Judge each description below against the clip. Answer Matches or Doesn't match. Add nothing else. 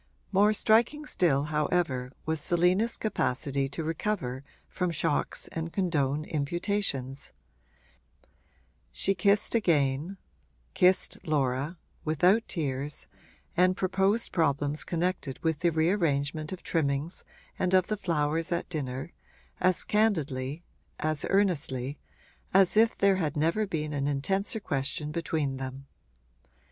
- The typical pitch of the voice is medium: Matches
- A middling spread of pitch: Matches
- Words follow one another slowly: Matches